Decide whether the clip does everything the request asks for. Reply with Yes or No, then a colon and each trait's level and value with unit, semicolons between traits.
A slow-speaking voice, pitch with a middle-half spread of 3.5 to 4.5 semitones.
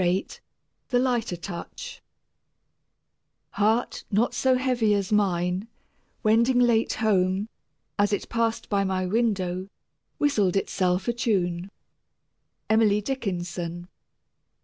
Yes: slow, 100 wpm; average, 3.9 semitones